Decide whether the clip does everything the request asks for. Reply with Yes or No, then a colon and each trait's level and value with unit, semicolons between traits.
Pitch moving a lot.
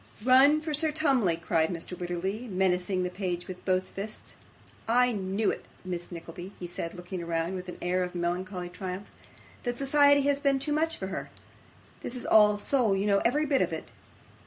Yes: wide, 6.0 semitones